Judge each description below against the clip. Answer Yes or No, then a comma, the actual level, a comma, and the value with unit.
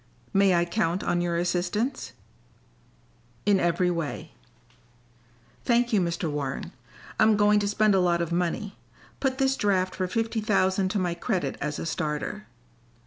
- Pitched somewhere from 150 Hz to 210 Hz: Yes, medium, 185 Hz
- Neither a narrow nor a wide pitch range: Yes, average, 3.5 semitones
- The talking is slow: No, average, 150 wpm